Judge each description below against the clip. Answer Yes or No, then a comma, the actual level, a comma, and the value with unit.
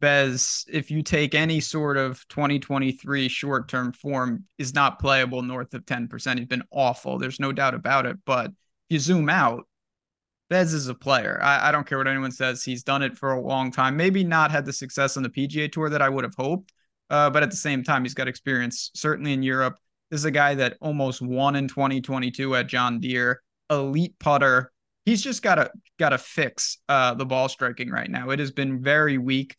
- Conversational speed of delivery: No, fast, 210 wpm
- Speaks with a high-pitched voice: No, low, 135 Hz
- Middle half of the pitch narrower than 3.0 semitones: Yes, narrow, 2.4 semitones